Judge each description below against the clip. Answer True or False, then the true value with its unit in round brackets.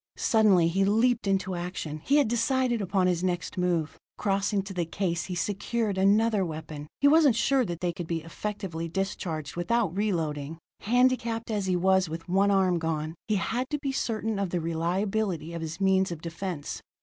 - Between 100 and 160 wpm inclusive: False (185 wpm)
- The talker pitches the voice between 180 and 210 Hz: True (190 Hz)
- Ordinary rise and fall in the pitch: True (4.4 semitones)